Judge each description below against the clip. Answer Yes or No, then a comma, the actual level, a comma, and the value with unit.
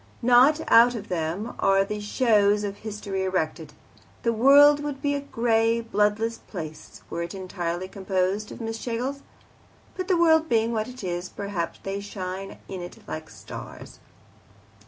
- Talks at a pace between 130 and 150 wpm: No, average, 160 wpm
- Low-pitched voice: No, high, 210 Hz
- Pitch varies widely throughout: No, average, 4.3 semitones